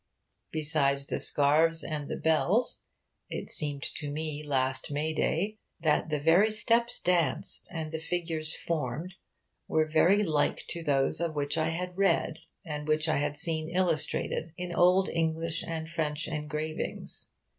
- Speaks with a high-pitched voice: No, medium, 160 Hz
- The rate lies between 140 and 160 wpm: Yes, average, 145 wpm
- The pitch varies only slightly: Yes, narrow, 2.2 semitones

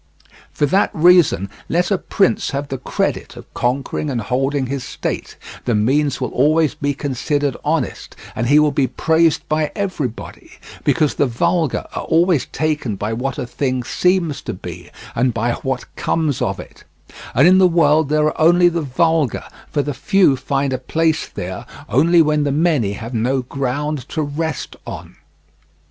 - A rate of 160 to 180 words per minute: Yes, average, 170 wpm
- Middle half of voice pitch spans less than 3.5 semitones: No, average, 3.9 semitones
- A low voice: No, medium, 145 Hz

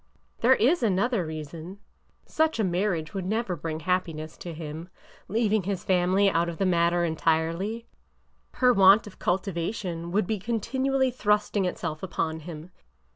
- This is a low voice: No, medium, 185 Hz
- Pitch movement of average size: Yes, average, 4.1 semitones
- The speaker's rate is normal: Yes, average, 155 wpm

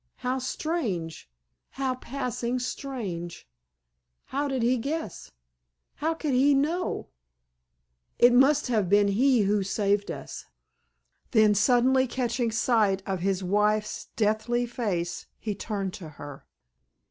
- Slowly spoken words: Yes, slow, 110 wpm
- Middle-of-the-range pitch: No, high, 215 Hz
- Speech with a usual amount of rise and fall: No, wide, 6.3 semitones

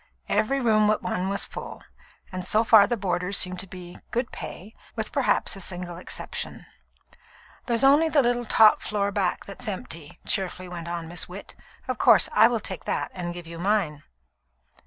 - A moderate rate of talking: Yes, average, 180 wpm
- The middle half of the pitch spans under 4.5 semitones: Yes, average, 3.7 semitones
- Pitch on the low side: No, high, 195 Hz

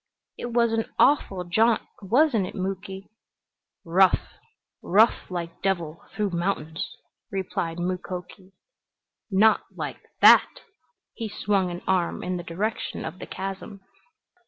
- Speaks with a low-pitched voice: No, high, 190 Hz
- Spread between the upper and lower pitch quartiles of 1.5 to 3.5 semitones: Yes, average, 3.1 semitones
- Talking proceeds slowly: Yes, slow, 120 wpm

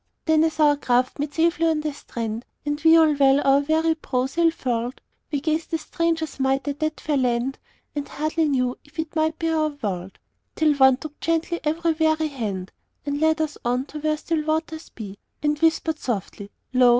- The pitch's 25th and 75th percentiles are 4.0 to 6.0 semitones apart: No, average, 3.1 semitones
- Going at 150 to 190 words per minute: No, average, 200 wpm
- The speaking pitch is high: Yes, very high, 300 Hz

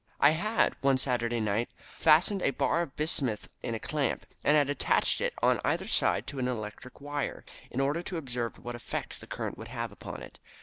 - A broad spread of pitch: No, average, 4.1 semitones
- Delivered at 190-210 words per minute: Yes, fast, 205 wpm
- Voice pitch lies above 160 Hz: No, low, 135 Hz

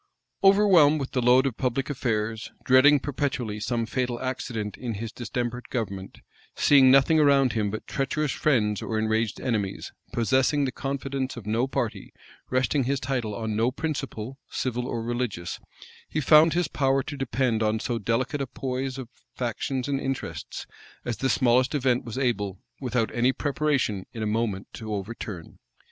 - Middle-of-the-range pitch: No, low, 125 Hz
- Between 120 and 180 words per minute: Yes, average, 160 wpm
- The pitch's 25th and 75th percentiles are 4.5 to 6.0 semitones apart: No, average, 3.4 semitones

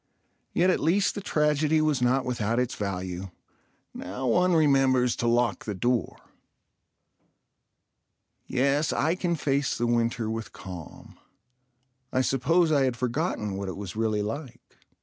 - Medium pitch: No, low, 125 Hz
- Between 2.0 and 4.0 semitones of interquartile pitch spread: No, average, 5.3 semitones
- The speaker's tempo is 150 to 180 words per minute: No, average, 140 wpm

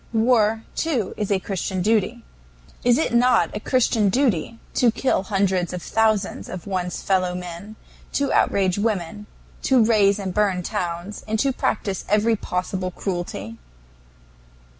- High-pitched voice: Yes, high, 205 Hz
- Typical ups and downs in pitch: Yes, average, 3.5 semitones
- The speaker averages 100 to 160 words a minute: Yes, average, 140 wpm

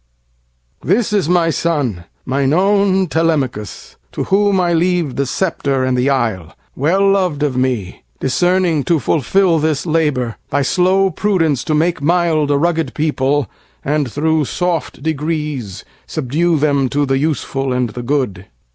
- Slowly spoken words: Yes, slow, 130 wpm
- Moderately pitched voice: Yes, medium, 150 Hz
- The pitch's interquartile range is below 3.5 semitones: No, average, 4.5 semitones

